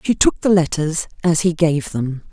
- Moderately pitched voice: Yes, medium, 160 Hz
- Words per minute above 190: Yes, fast, 205 wpm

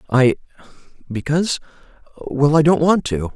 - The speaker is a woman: No, male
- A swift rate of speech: No, slow, 90 wpm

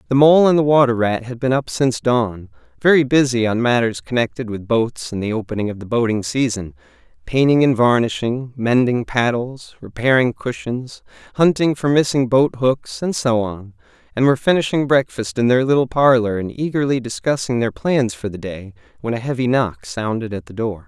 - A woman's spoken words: No, male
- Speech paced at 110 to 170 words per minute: No, average, 185 wpm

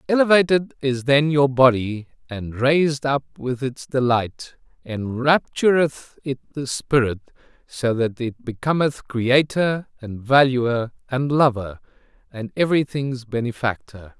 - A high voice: No, low, 130 Hz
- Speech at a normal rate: No, slow, 115 wpm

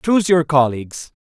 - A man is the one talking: Yes, male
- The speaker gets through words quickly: No, average, 145 wpm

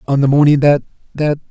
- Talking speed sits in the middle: Yes, average, 160 wpm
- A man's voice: Yes, male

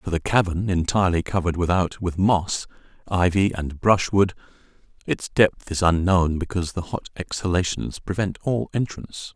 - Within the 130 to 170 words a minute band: Yes, average, 145 wpm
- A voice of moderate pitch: No, very low, 90 Hz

